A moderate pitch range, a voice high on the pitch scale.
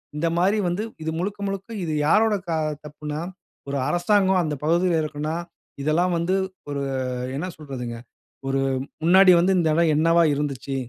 No: average, 3.5 semitones; medium, 165 Hz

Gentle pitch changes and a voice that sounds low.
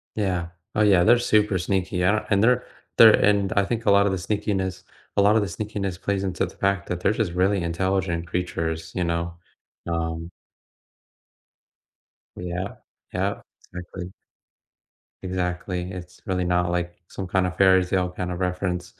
Yes: narrow, 2.1 semitones; very low, 95 Hz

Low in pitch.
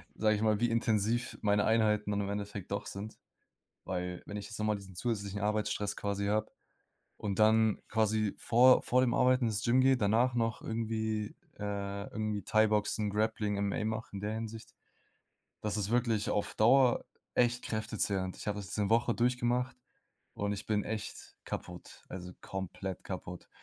Yes: low, 110 Hz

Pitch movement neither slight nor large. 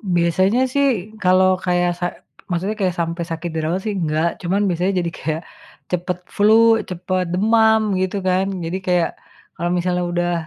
No: narrow, 2.1 semitones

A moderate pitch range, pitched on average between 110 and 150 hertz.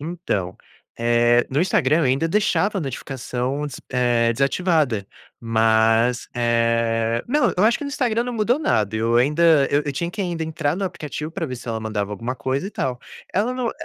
No: wide, 6.7 semitones; low, 135 Hz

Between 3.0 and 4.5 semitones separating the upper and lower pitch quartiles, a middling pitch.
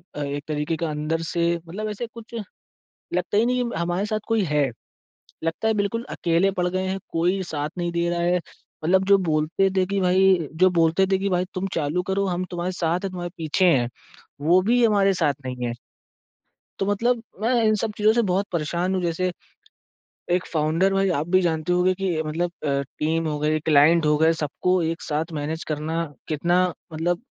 Yes: average, 3.3 semitones; medium, 175 Hz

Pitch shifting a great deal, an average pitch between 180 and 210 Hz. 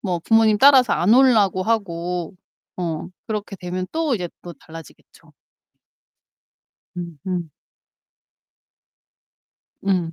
No: average, 4.3 semitones; medium, 185 Hz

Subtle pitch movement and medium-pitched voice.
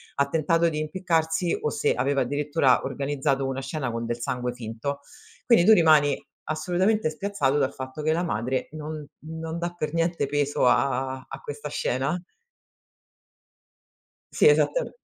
No: average, 3.5 semitones; medium, 145 Hz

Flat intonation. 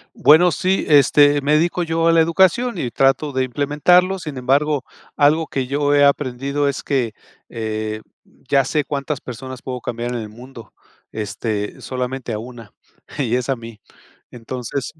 No: average, 3.5 semitones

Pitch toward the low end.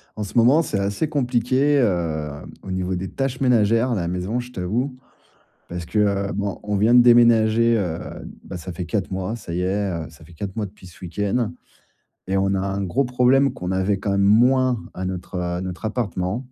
Yes: low, 100 Hz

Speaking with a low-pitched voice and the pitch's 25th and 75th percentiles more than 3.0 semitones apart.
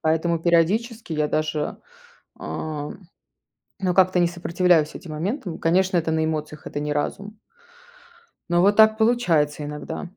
No: medium, 170 Hz; average, 3.6 semitones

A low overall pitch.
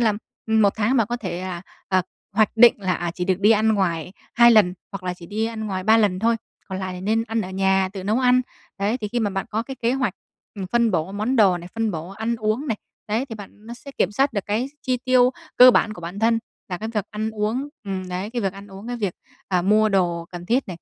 No: high, 210 Hz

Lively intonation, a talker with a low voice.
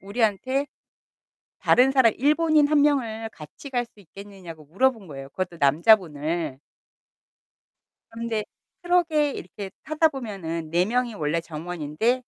No: wide, 7.9 semitones; high, 215 Hz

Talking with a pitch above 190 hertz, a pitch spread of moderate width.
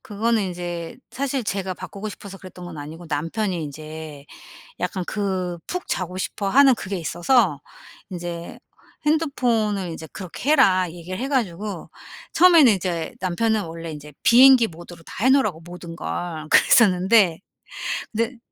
No: medium, 185 Hz; average, 5.0 semitones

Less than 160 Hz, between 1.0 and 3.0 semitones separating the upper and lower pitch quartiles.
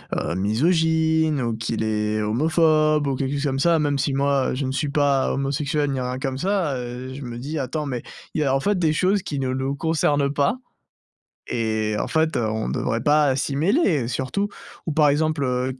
No: medium, 140 Hz; average, 3.4 semitones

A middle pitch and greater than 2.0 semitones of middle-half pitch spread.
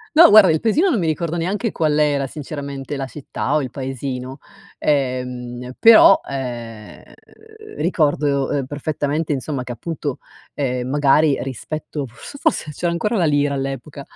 Yes: medium, 145 Hz; average, 2.9 semitones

